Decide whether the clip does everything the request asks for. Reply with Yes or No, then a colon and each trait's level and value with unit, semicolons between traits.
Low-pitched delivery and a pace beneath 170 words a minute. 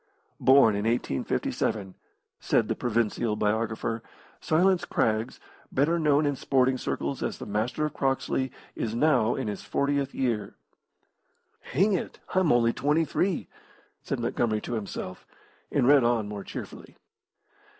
Yes: low, 120 Hz; slow, 135 wpm